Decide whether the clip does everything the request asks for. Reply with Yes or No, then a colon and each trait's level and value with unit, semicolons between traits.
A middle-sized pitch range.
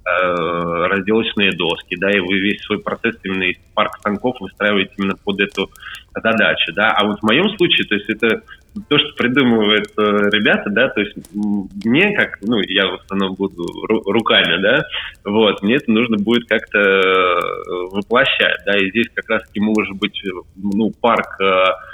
No: narrow, 2.2 semitones